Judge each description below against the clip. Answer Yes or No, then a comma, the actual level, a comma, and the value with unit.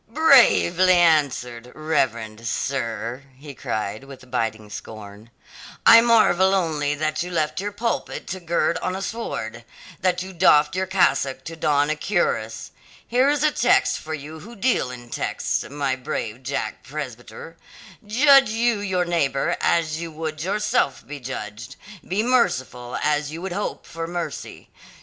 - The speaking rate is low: No, average, 150 wpm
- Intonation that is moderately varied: No, wide, 6.6 semitones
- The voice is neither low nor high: Yes, medium, 155 Hz